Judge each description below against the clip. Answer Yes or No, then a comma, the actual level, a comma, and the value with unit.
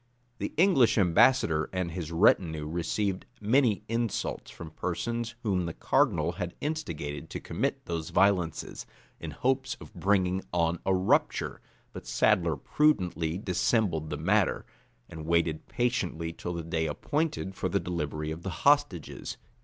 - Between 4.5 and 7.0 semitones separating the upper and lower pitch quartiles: Yes, wide, 5.5 semitones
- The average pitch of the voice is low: Yes, very low, 90 Hz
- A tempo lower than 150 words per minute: Yes, average, 140 wpm